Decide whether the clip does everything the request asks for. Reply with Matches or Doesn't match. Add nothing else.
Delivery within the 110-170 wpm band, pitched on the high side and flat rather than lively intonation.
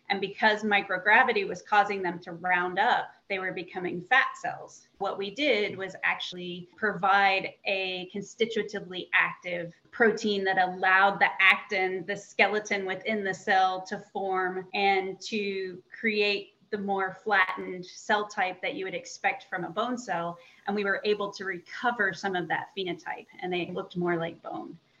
Matches